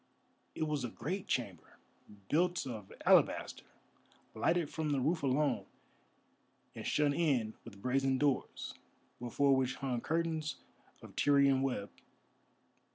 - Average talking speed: No, slow, 120 wpm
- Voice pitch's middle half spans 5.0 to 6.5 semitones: No, average, 3.4 semitones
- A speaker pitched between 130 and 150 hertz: Yes, medium, 140 Hz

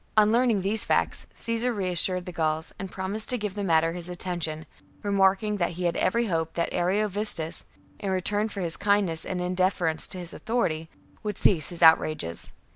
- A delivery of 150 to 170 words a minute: No, average, 195 wpm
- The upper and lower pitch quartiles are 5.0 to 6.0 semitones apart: No, average, 3.6 semitones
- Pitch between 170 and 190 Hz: Yes, medium, 185 Hz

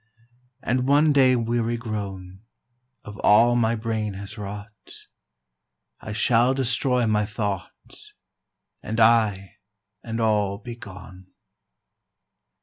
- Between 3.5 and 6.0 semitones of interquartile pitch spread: No, average, 2.7 semitones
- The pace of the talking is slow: Yes, slow, 105 wpm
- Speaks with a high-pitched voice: No, low, 110 Hz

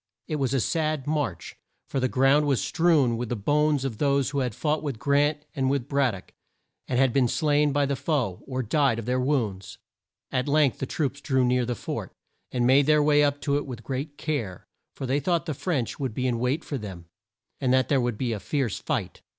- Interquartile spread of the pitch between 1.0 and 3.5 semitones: Yes, average, 2.9 semitones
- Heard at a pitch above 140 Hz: No, low, 135 Hz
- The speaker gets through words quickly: Yes, fast, 225 wpm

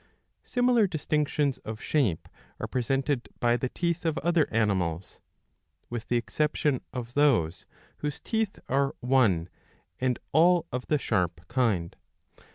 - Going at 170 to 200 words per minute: No, slow, 135 wpm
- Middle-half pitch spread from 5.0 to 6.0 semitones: Yes, average, 5.3 semitones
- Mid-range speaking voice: No, low, 130 Hz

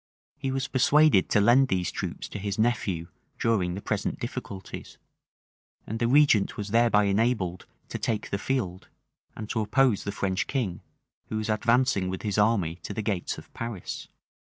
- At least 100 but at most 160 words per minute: No, average, 170 wpm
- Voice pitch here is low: Yes, low, 105 Hz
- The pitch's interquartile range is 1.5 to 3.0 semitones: No, average, 3.7 semitones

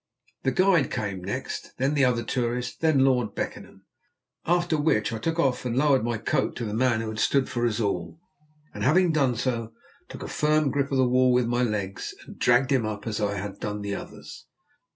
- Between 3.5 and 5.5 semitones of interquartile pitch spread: Yes, average, 4.1 semitones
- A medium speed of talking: No, fast, 215 wpm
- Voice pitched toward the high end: No, low, 125 Hz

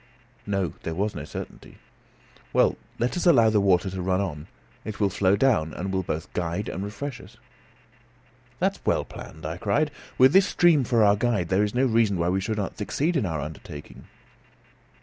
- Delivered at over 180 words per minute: Yes, average, 195 wpm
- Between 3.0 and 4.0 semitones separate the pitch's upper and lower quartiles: No, average, 4.7 semitones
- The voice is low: Yes, low, 100 Hz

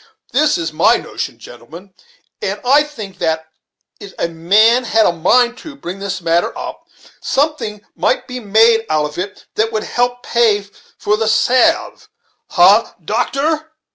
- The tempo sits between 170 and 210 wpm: No, average, 155 wpm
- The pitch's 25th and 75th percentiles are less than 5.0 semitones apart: No, wide, 5.6 semitones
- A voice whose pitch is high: Yes, high, 220 Hz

